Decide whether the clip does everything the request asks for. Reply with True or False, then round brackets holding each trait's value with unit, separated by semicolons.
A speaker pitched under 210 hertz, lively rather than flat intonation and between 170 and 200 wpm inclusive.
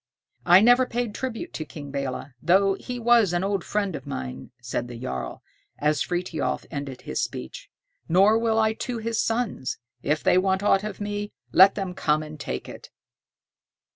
True (190 Hz; 6.6 semitones; 175 wpm)